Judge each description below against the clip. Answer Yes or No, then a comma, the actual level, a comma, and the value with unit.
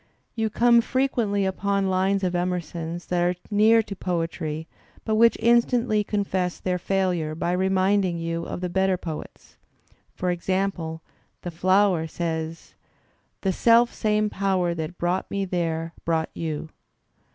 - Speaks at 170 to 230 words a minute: No, average, 140 wpm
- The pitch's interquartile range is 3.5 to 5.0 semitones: No, average, 3.0 semitones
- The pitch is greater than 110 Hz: Yes, medium, 185 Hz